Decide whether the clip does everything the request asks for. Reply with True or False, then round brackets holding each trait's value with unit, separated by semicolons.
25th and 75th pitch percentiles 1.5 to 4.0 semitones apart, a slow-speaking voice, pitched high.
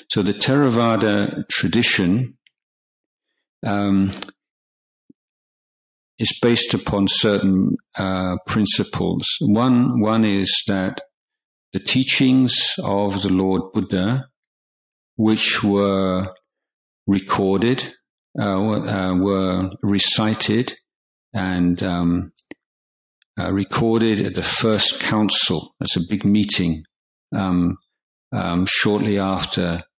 False (2.7 semitones; 90 wpm; 100 Hz)